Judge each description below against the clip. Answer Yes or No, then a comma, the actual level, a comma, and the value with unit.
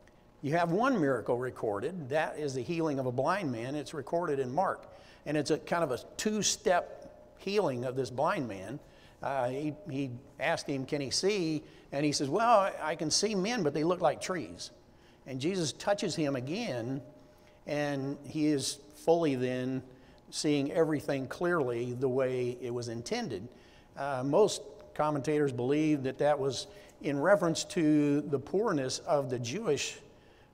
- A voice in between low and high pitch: Yes, medium, 145 Hz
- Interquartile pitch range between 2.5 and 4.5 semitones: Yes, average, 3.5 semitones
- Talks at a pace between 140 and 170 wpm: Yes, average, 165 wpm